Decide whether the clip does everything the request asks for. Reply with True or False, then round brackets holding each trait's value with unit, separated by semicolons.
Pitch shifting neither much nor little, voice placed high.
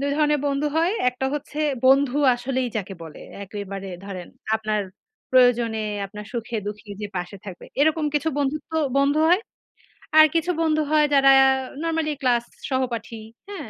False (6.0 semitones; 260 Hz)